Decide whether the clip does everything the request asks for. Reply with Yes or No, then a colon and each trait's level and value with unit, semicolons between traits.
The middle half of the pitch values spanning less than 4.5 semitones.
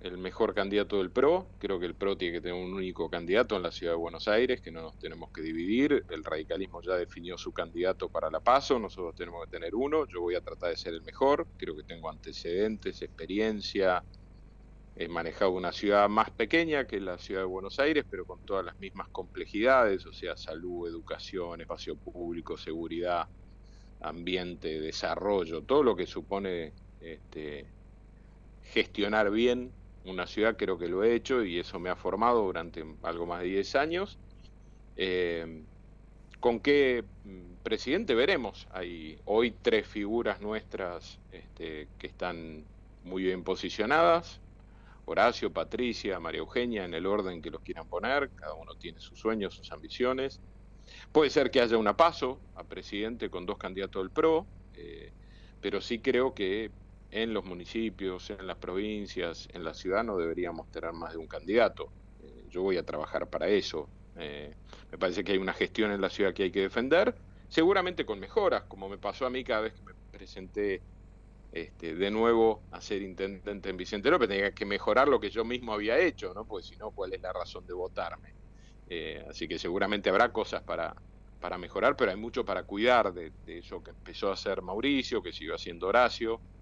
Yes: average, 3.4 semitones